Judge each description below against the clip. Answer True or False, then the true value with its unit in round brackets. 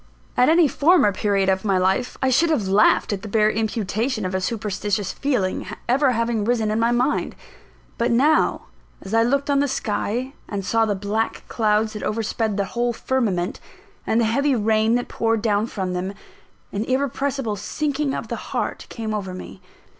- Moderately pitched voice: False (225 Hz)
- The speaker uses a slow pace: False (185 wpm)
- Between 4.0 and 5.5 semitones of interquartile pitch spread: False (3.6 semitones)